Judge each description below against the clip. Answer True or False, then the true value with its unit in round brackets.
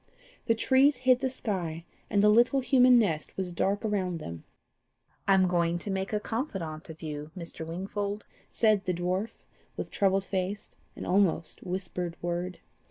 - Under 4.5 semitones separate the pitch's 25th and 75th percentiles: True (3.7 semitones)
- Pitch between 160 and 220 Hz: True (190 Hz)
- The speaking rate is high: False (165 wpm)